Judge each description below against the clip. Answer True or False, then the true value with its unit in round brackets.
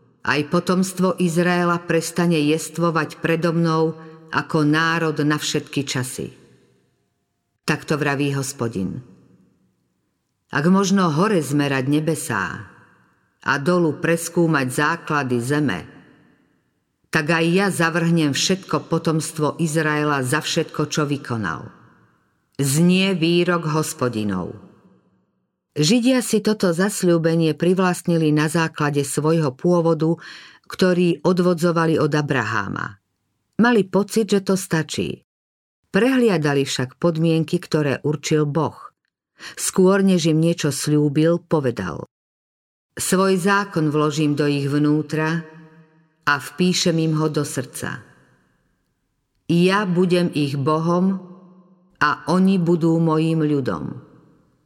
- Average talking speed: False (100 wpm)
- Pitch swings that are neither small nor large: True (3.1 semitones)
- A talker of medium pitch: True (160 Hz)